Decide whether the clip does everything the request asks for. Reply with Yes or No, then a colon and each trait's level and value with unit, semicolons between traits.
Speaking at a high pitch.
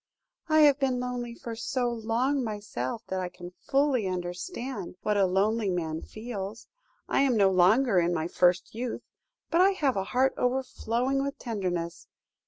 Yes: high, 225 Hz